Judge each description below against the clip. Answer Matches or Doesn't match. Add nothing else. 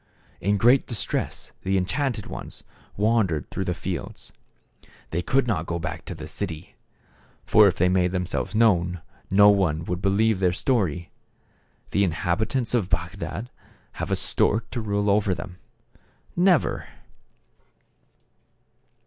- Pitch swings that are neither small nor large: Matches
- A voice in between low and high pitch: Doesn't match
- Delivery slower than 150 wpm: Matches